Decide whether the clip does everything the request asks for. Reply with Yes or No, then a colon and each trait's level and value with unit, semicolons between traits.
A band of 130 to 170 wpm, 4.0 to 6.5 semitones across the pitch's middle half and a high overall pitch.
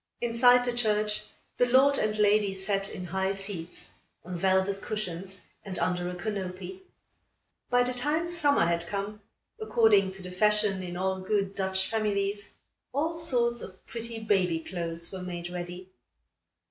No: average, 150 wpm; average, 3.6 semitones; high, 195 Hz